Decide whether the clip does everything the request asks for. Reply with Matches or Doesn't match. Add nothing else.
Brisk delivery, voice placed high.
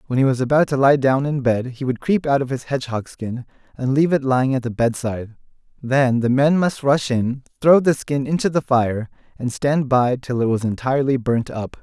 Doesn't match